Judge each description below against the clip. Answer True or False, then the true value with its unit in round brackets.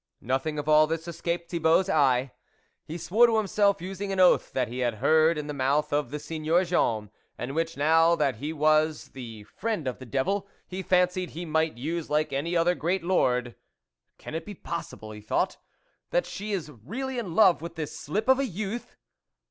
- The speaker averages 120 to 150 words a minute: False (205 wpm)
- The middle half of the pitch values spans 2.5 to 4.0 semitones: False (4.4 semitones)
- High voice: False (160 Hz)